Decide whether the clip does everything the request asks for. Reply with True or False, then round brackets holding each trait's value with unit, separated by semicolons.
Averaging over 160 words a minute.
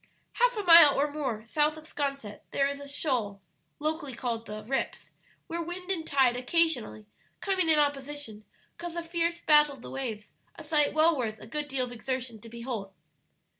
True (185 wpm)